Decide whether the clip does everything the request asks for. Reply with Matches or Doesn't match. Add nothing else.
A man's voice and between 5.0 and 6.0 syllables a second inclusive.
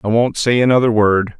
Matches